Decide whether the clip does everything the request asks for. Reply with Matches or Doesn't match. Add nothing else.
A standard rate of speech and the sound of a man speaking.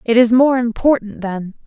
Doesn't match